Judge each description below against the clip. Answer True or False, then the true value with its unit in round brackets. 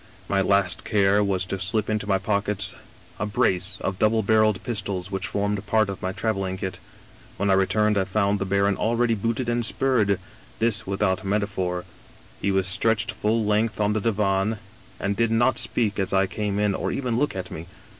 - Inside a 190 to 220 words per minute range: True (195 wpm)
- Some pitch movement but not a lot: False (2.0 semitones)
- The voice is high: False (100 Hz)